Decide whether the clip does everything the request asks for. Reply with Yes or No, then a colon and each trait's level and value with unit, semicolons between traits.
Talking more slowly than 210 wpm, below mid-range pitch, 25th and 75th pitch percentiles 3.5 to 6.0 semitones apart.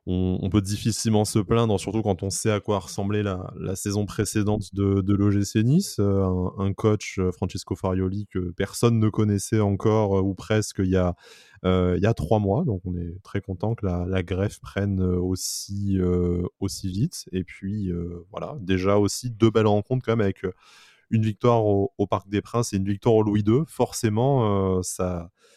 No: average, 200 wpm; low, 100 Hz; narrow, 2.6 semitones